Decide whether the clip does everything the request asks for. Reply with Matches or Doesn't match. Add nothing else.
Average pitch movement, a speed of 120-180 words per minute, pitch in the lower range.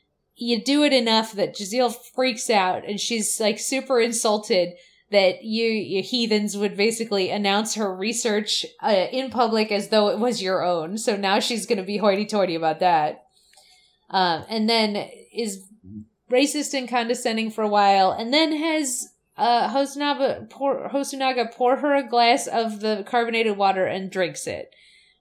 Doesn't match